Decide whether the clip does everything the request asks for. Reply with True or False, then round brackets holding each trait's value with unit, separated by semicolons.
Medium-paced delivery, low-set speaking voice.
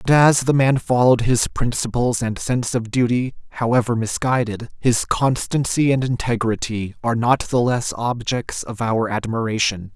True (150 wpm; 120 Hz)